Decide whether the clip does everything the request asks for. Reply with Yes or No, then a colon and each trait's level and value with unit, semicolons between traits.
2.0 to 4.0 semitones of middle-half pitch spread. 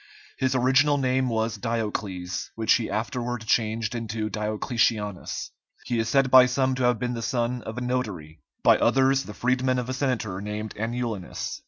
Yes: average, 2.8 semitones